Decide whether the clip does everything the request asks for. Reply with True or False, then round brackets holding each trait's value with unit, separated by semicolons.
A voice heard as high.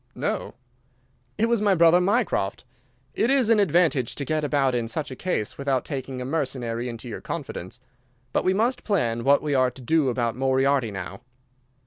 False (140 Hz)